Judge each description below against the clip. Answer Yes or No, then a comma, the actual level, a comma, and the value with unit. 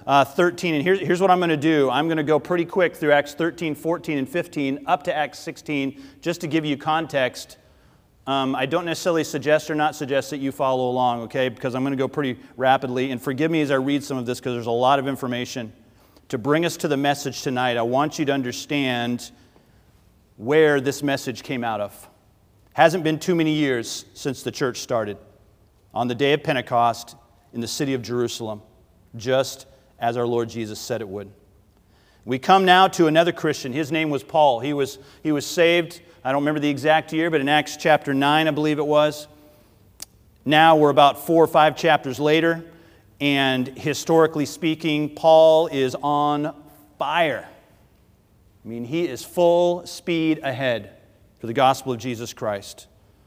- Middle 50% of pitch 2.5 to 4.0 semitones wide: No, average, 4.4 semitones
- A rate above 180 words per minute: Yes, average, 190 wpm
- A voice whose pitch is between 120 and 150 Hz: Yes, medium, 140 Hz